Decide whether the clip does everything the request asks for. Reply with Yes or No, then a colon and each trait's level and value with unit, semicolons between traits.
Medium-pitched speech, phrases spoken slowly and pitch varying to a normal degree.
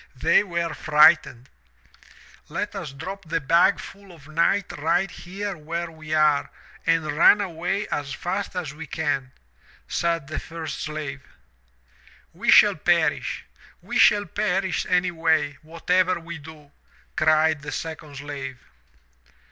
Yes: medium, 160 Hz; slow, 130 wpm; average, 3.0 semitones